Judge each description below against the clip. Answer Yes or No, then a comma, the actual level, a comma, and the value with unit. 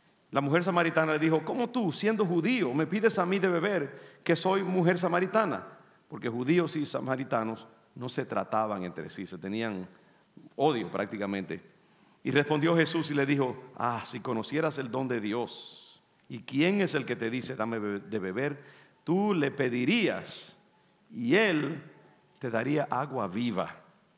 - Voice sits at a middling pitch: Yes, medium, 145 Hz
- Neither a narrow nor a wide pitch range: No, wide, 7.4 semitones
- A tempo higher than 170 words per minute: No, average, 160 wpm